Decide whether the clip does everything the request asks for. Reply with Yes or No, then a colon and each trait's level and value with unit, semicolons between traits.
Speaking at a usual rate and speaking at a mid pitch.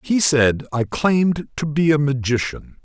Yes: average, 170 wpm; medium, 145 Hz